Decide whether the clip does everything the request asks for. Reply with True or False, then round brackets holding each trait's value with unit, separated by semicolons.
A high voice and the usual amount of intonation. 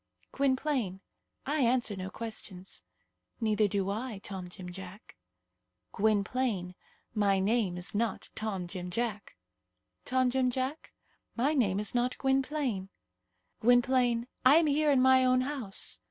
True (230 Hz; 5.0 semitones)